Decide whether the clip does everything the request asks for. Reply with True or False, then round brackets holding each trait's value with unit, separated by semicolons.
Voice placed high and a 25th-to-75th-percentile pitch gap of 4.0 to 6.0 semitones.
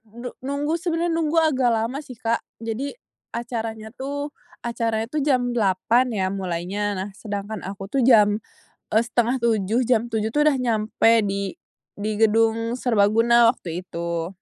False (230 Hz; 3.4 semitones)